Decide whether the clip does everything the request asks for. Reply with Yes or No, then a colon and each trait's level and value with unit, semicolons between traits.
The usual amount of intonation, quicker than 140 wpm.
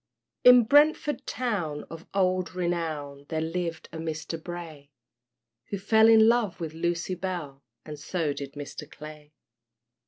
No: average, 4.0 semitones; slow, 135 wpm